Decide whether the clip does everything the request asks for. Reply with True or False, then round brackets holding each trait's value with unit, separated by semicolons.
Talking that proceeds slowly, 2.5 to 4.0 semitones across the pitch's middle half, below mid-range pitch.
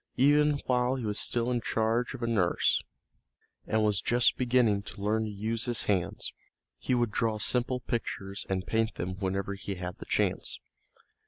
False (175 wpm; 3.6 semitones; 110 Hz)